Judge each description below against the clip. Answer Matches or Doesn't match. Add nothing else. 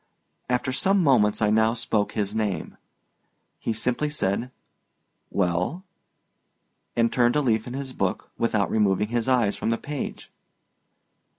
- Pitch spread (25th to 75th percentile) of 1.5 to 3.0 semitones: Doesn't match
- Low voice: Matches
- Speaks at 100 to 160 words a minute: Matches